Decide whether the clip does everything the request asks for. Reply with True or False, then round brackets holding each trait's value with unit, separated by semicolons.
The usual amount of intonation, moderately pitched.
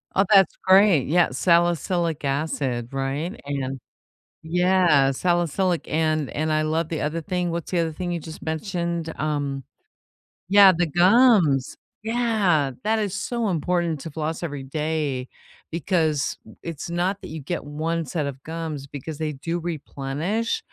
True (3.5 semitones; 165 Hz)